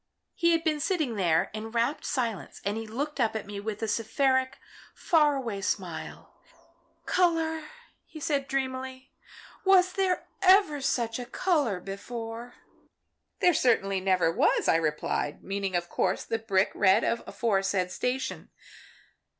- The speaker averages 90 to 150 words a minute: Yes, average, 145 wpm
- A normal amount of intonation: No, wide, 6.7 semitones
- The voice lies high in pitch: Yes, high, 235 Hz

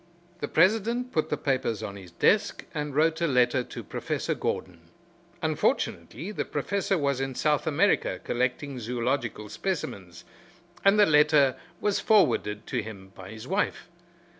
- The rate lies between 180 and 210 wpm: No, average, 145 wpm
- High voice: No, low, 135 Hz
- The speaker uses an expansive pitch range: Yes, wide, 6.9 semitones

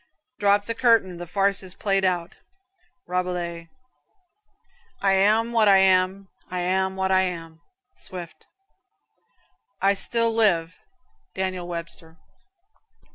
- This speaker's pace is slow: Yes, slow, 115 wpm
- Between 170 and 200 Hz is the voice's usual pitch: Yes, high, 190 Hz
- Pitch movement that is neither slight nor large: No, narrow, 2.1 semitones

